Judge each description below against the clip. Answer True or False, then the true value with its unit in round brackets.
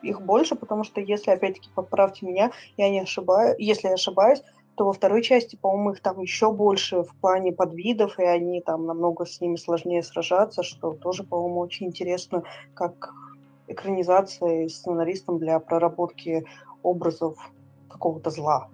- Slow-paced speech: False (150 wpm)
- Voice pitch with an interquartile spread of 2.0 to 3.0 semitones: True (2.5 semitones)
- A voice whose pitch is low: False (180 Hz)